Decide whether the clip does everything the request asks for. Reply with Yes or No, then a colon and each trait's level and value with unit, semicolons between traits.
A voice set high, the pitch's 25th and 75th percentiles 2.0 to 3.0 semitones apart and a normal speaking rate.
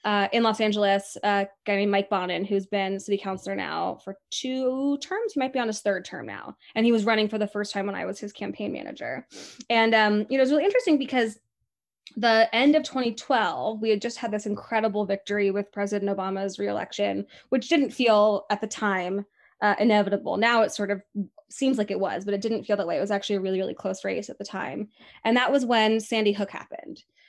No: high, 210 Hz; narrow, 2.6 semitones; fast, 230 wpm